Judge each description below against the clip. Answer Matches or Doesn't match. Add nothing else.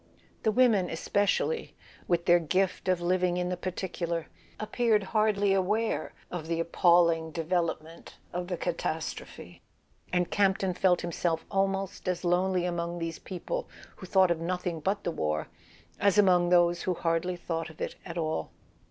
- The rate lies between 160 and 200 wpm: Doesn't match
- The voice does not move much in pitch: Matches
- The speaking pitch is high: Doesn't match